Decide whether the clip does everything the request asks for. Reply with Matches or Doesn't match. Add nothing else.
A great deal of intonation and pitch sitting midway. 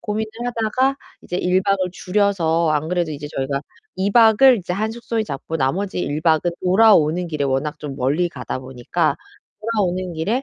Matches